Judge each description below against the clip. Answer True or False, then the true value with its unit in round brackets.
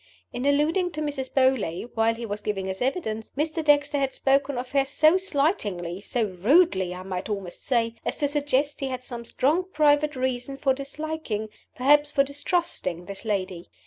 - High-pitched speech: True (270 Hz)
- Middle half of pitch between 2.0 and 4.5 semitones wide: False (5.2 semitones)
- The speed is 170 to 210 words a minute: True (175 wpm)